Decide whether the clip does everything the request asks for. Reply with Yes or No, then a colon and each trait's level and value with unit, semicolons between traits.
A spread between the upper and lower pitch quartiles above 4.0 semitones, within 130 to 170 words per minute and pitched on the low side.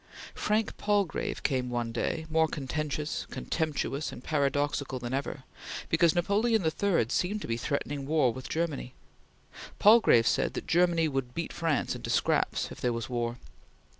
No: average, 4.7 semitones; average, 150 wpm; medium, 150 Hz